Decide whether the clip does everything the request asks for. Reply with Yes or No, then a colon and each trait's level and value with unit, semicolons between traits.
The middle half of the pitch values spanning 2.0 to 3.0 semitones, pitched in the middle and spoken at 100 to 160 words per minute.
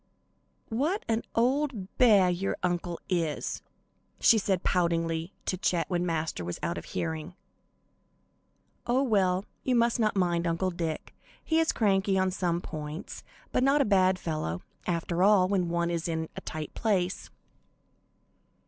No: average, 3.8 semitones; medium, 180 Hz; average, 150 wpm